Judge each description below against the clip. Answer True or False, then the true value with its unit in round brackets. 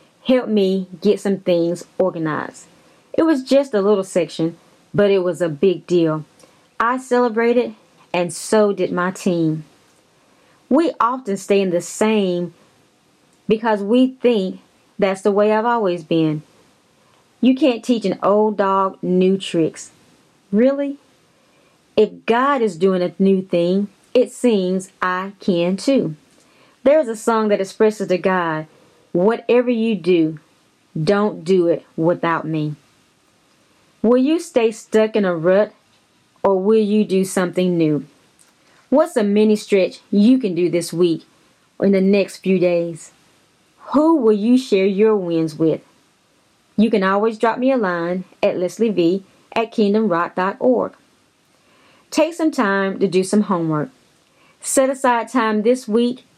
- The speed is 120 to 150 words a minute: True (145 wpm)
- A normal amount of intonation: True (4.4 semitones)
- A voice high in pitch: True (195 Hz)